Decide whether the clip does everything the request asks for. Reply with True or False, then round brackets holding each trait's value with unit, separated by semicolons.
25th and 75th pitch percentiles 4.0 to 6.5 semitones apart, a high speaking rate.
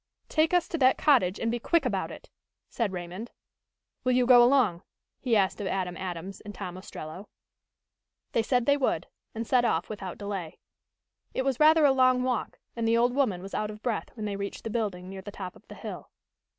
True (5.0 semitones; 210 wpm)